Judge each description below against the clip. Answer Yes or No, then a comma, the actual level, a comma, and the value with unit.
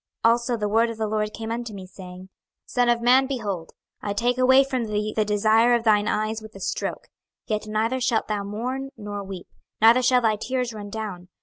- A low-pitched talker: No, high, 220 Hz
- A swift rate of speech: Yes, fast, 220 wpm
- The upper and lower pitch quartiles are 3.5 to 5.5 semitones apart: No, narrow, 2.5 semitones